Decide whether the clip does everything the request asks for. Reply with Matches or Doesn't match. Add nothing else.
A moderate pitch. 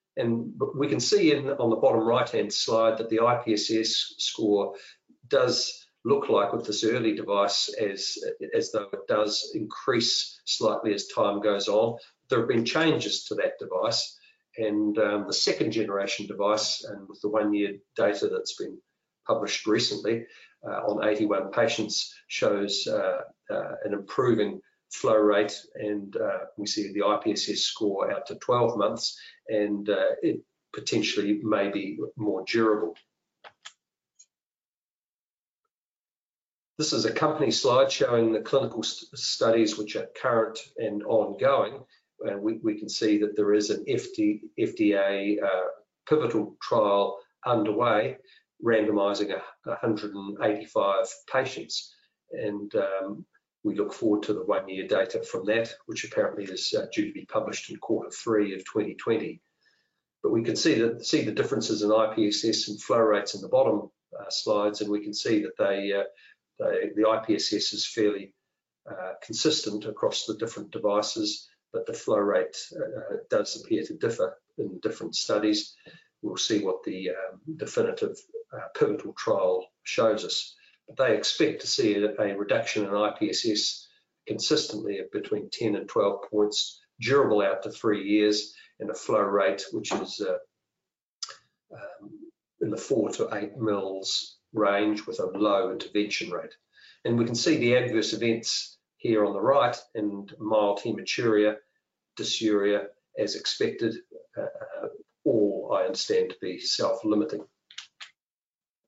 Doesn't match